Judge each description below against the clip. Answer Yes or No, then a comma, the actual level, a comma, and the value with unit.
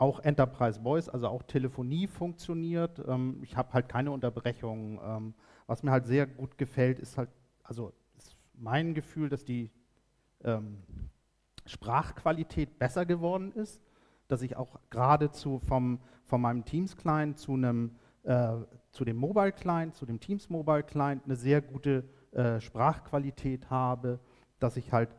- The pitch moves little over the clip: No, average, 3.4 semitones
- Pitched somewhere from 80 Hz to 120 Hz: No, low, 130 Hz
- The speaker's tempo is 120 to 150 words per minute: Yes, average, 140 wpm